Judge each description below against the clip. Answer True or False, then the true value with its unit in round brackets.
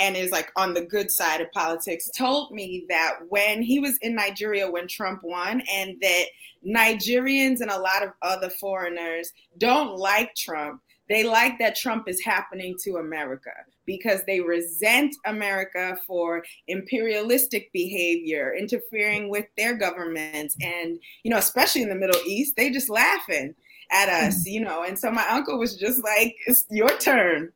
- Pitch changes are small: False (4.2 semitones)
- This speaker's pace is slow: False (165 wpm)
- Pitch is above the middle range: True (195 Hz)